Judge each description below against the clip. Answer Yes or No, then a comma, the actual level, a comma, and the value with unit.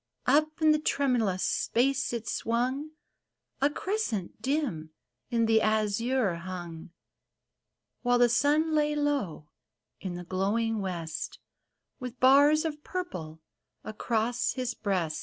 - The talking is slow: Yes, slow, 120 wpm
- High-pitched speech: Yes, high, 235 Hz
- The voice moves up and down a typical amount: No, wide, 7.1 semitones